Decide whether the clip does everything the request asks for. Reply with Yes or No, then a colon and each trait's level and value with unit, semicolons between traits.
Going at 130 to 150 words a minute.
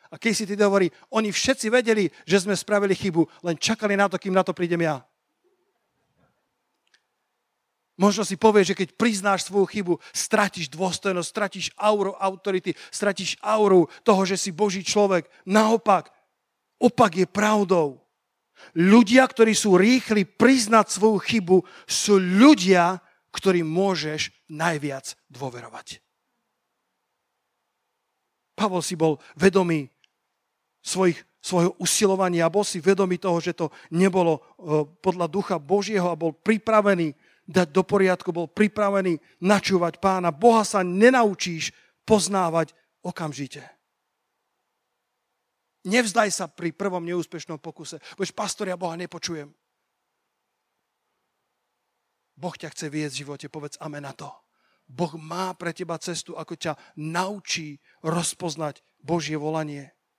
No: average, 120 wpm